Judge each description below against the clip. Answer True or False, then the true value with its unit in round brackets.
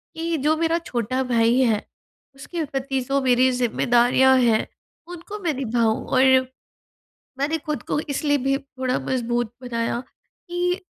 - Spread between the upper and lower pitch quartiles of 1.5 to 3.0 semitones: False (4.1 semitones)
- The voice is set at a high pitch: True (265 Hz)